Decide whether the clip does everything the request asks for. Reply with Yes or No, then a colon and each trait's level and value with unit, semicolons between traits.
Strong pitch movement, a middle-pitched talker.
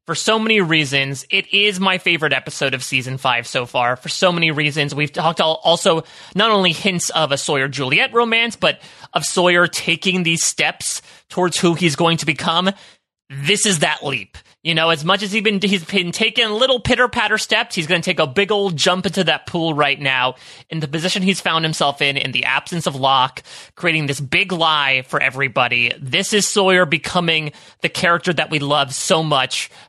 No: average, 4.8 semitones; medium, 170 Hz